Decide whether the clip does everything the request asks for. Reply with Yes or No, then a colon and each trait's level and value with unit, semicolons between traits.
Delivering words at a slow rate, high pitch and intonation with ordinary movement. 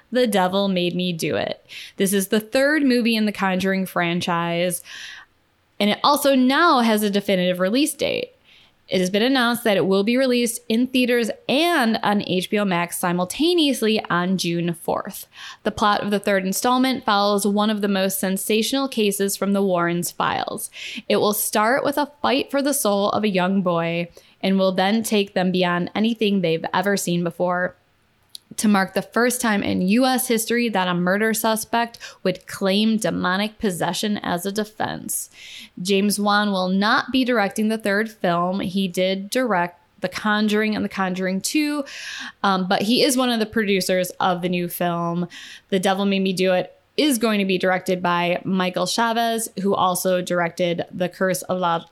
No: average, 180 wpm; high, 200 Hz; average, 3.7 semitones